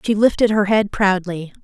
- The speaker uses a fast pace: No, average, 185 wpm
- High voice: Yes, high, 200 Hz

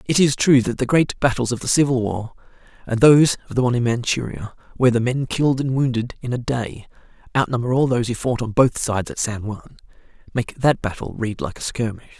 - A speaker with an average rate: No, fast, 220 wpm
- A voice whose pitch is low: Yes, low, 125 Hz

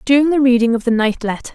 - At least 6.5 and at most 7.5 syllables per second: Yes, 6.9 syllables/s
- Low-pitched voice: No, high, 245 Hz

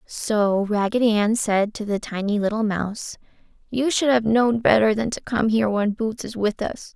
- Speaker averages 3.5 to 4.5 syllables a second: No, 4.8 syllables/s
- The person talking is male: No, female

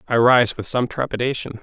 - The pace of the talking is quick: No, average, 185 wpm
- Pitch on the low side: Yes, low, 120 Hz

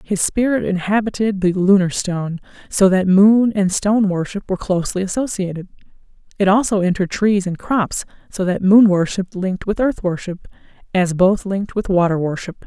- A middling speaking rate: Yes, average, 165 wpm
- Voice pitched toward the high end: Yes, high, 195 Hz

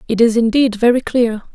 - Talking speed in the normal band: Yes, average, 195 wpm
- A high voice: Yes, high, 230 Hz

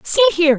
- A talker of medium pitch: No, very high, 345 Hz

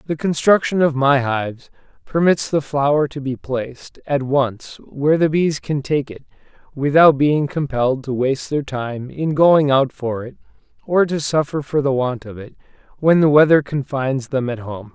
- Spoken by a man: Yes, male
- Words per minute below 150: No, average, 185 wpm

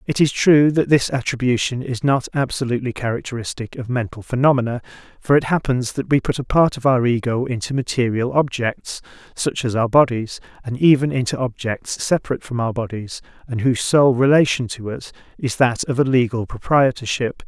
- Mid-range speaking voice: No, low, 125 Hz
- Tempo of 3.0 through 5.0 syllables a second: No, 5.5 syllables/s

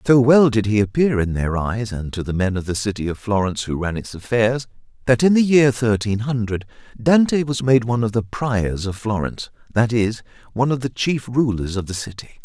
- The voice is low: Yes, low, 115 Hz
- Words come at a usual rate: No, fast, 220 wpm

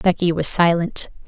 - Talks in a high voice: No, medium, 170 Hz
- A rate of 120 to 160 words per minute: Yes, average, 140 wpm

